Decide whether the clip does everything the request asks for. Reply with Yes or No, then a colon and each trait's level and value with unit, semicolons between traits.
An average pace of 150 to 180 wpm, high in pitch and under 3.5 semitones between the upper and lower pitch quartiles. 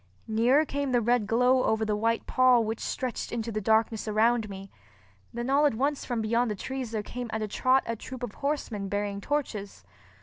No: fast, 205 wpm; high, 230 Hz; average, 3.0 semitones